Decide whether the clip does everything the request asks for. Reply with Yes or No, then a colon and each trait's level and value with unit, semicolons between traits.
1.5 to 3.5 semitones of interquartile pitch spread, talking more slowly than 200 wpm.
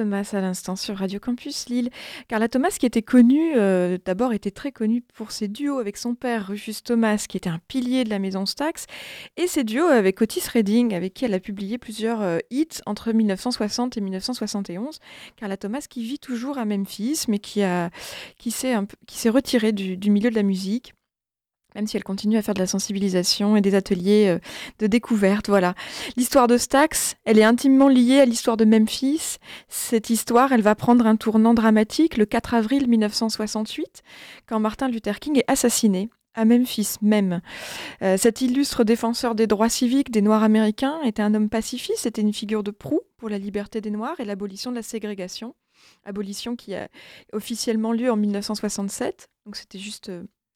Yes: average, 3.2 semitones; average, 190 wpm